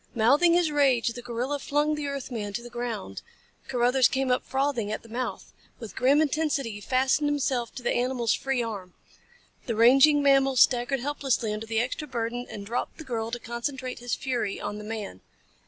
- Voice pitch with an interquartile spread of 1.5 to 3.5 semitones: Yes, average, 3.1 semitones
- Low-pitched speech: No, high, 245 Hz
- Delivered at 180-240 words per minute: Yes, average, 190 wpm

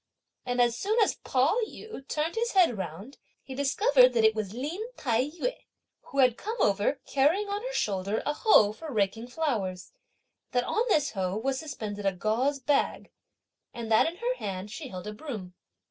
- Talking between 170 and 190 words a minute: Yes, average, 185 wpm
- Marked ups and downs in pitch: Yes, wide, 6.9 semitones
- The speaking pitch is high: Yes, very high, 255 Hz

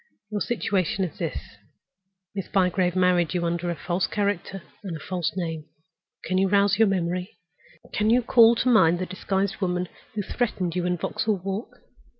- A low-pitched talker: No, medium, 185 Hz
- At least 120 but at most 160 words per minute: No, average, 175 wpm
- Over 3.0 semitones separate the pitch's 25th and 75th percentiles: No, narrow, 2.4 semitones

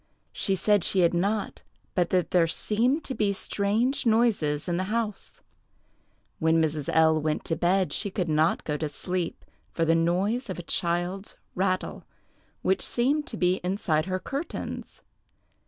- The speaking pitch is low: No, medium, 185 Hz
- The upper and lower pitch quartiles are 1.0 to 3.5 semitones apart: No, average, 4.1 semitones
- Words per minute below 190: Yes, average, 160 wpm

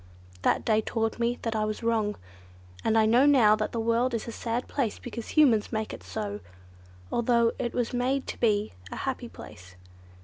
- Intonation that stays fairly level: Yes, narrow, 2.1 semitones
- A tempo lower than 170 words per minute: No, average, 190 wpm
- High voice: Yes, high, 230 Hz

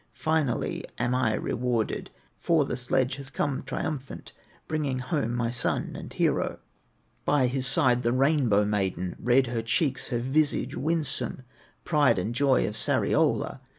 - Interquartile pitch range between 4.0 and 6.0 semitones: No, average, 3.0 semitones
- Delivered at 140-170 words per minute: Yes, average, 145 wpm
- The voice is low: Yes, low, 130 Hz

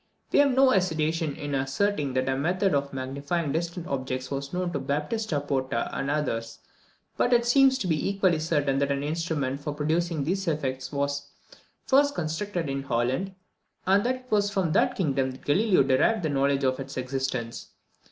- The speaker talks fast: No, average, 180 wpm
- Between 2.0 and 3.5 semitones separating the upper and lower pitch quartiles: No, average, 5.2 semitones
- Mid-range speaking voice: Yes, medium, 150 Hz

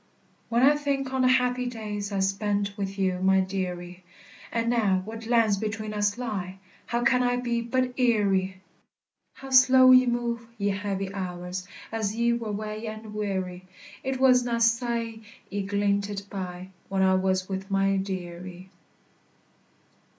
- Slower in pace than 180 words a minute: Yes, average, 155 wpm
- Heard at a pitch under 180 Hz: No, high, 210 Hz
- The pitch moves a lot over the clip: No, average, 3.7 semitones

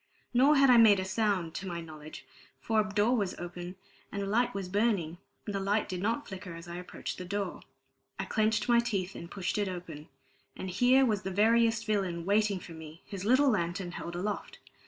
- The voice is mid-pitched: No, high, 200 Hz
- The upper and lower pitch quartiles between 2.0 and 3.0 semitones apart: No, average, 3.7 semitones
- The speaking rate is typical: No, fast, 210 wpm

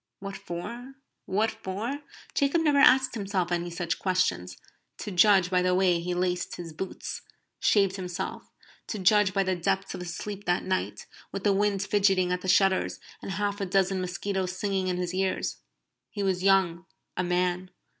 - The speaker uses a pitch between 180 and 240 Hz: Yes, high, 190 Hz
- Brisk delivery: No, average, 175 wpm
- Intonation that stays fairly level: Yes, narrow, 1.9 semitones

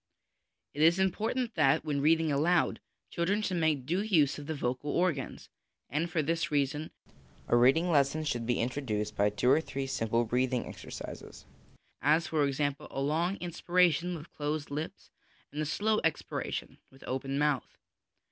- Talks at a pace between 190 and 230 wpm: No, average, 165 wpm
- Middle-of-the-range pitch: Yes, medium, 150 Hz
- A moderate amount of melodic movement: Yes, average, 3.7 semitones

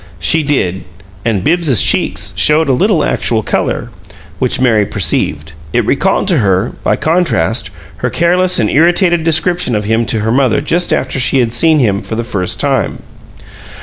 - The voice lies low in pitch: Yes, low, 130 Hz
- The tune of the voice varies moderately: No, wide, 6.9 semitones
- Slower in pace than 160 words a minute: No, average, 170 wpm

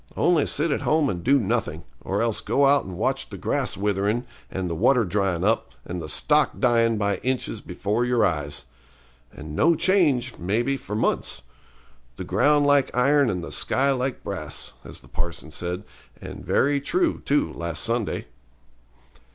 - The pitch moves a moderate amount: No, wide, 6.7 semitones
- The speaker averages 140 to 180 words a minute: Yes, average, 170 wpm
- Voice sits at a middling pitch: No, low, 115 Hz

